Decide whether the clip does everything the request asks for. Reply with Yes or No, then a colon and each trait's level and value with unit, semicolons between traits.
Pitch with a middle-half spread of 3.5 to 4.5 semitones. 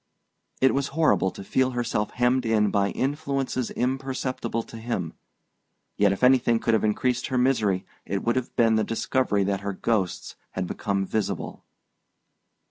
Yes: average, 4.1 semitones